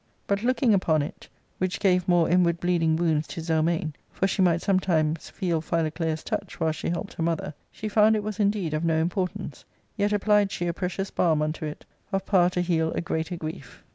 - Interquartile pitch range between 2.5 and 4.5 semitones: Yes, average, 3.2 semitones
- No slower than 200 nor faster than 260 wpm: Yes, fast, 205 wpm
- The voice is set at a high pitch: No, medium, 175 Hz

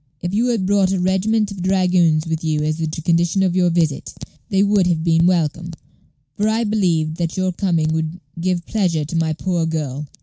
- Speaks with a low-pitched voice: No, medium, 175 Hz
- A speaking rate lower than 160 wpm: No, average, 200 wpm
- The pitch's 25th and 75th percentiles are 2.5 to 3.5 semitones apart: Yes, average, 3.0 semitones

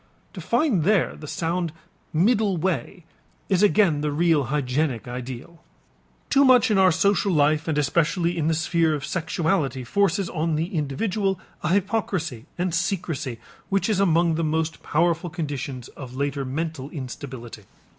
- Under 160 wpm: Yes, average, 150 wpm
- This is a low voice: No, medium, 165 Hz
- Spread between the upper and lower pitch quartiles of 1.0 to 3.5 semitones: No, average, 4.5 semitones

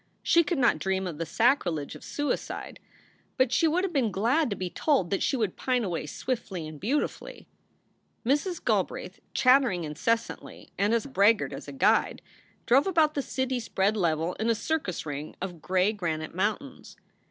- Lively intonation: Yes, wide, 7.0 semitones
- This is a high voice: Yes, high, 220 Hz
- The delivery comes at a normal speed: Yes, average, 175 wpm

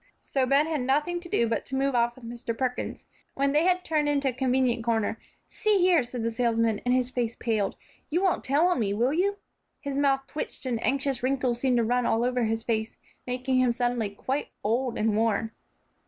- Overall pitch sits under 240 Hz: No, very high, 250 Hz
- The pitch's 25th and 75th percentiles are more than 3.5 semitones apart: No, average, 3.1 semitones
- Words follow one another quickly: Yes, fast, 215 wpm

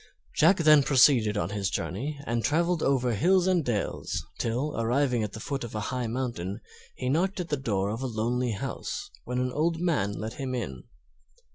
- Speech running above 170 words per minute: Yes, average, 190 wpm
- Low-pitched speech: Yes, low, 125 Hz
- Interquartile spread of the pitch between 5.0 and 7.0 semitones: Yes, wide, 5.4 semitones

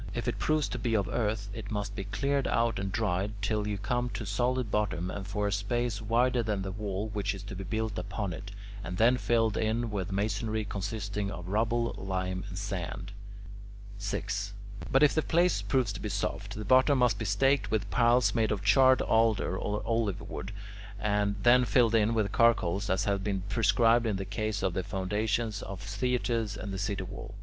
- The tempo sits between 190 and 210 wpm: Yes, average, 200 wpm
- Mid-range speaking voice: No, low, 105 Hz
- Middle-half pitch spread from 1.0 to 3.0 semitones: Yes, narrow, 2.6 semitones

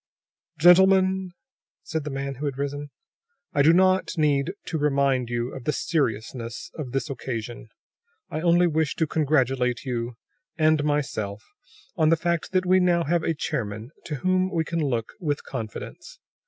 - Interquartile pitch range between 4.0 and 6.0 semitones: Yes, average, 4.9 semitones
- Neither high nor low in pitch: Yes, medium, 150 Hz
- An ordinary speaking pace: Yes, average, 160 wpm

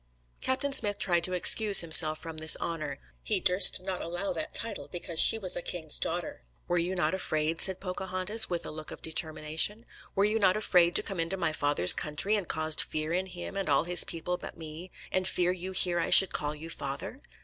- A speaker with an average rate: No, fast, 215 wpm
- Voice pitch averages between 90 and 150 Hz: No, medium, 175 Hz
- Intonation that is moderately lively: Yes, average, 3.1 semitones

